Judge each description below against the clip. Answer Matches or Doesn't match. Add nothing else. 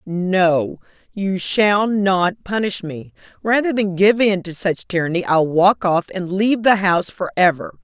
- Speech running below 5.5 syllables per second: Matches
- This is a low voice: Doesn't match